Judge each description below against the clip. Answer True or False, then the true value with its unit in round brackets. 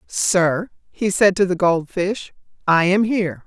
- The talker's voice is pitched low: False (190 Hz)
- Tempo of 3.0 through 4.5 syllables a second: True (3.9 syllables/s)